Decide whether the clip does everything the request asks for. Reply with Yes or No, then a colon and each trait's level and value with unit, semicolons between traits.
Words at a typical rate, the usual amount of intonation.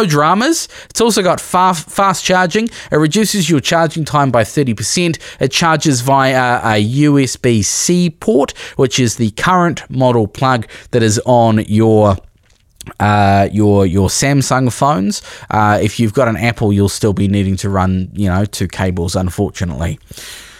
No: average, 155 wpm; wide, 6.8 semitones